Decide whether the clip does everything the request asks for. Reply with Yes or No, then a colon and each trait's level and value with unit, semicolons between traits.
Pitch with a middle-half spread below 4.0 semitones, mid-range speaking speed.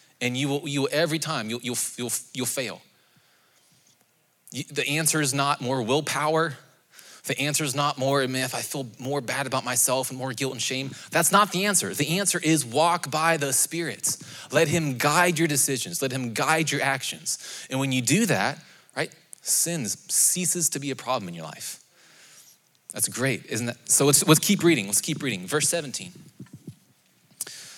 Yes: average, 3.6 semitones; average, 190 wpm